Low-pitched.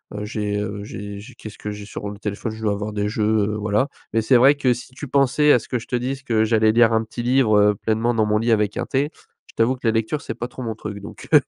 Yes: low, 110 Hz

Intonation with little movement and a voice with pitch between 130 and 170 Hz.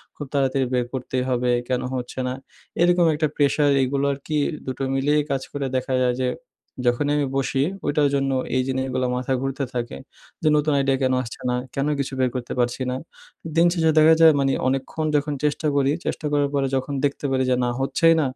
Yes: narrow, 2.1 semitones; low, 135 Hz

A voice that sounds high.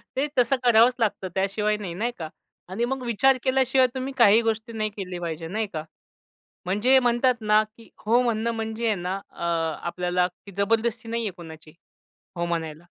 Yes: high, 220 Hz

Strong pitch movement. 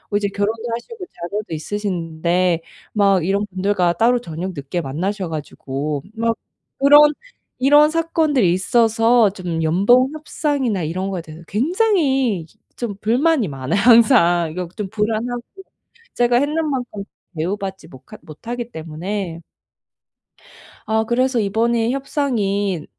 Yes: wide, 5.8 semitones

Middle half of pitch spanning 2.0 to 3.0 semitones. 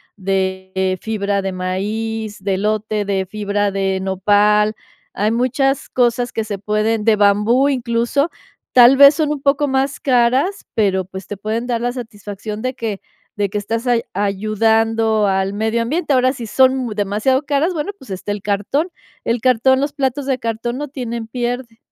No: average, 3.9 semitones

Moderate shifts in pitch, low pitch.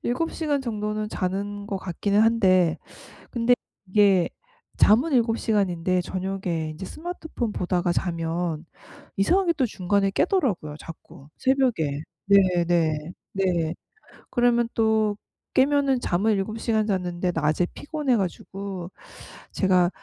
No: average, 4.7 semitones; high, 200 Hz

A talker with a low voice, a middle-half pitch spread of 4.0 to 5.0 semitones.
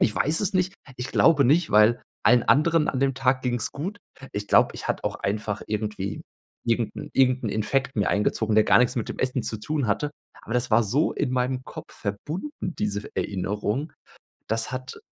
Yes: low, 125 Hz; average, 4.6 semitones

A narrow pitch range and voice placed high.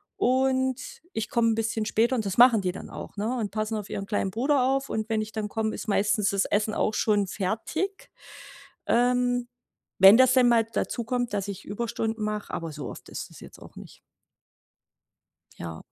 No: average, 3.1 semitones; high, 220 Hz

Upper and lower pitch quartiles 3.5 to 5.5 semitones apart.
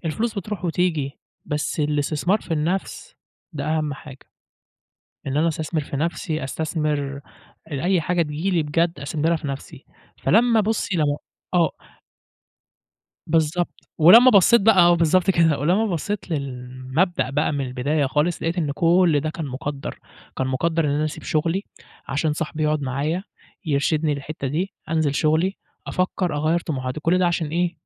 No: average, 3.1 semitones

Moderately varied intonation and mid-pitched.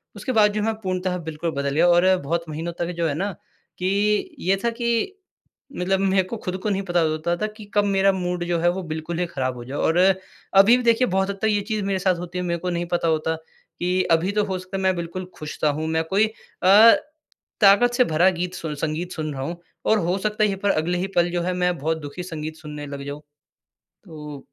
Yes: average, 3.3 semitones; medium, 180 Hz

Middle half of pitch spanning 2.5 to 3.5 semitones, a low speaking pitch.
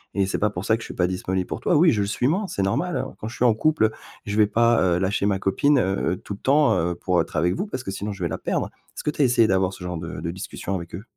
No: average, 4.3 semitones; low, 100 Hz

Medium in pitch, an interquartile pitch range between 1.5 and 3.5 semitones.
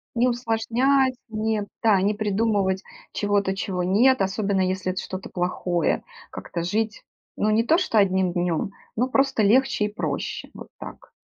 No: high, 210 Hz; average, 3.2 semitones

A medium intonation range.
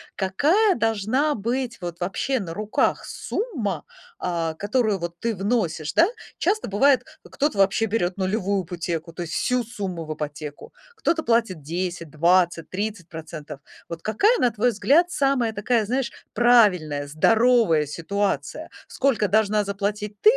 No: wide, 5.8 semitones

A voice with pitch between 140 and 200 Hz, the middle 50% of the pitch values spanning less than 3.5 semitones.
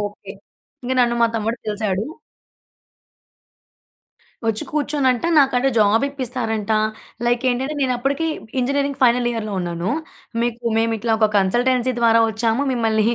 No: high, 235 Hz; average, 2.8 semitones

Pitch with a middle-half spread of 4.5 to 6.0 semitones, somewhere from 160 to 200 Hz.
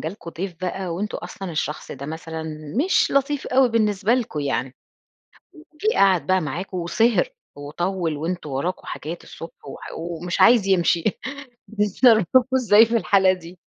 Yes: average, 5.1 semitones; medium, 185 Hz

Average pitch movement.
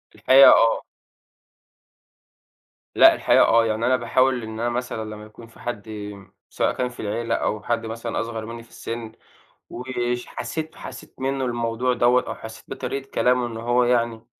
No: narrow, 1.6 semitones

